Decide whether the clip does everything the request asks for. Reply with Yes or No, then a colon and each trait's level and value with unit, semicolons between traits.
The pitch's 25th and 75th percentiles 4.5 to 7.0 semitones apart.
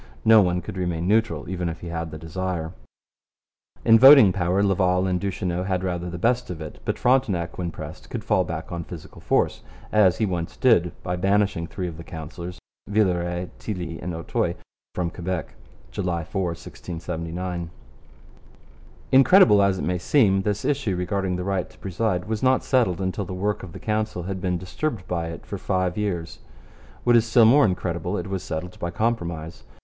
No: average, 3.0 semitones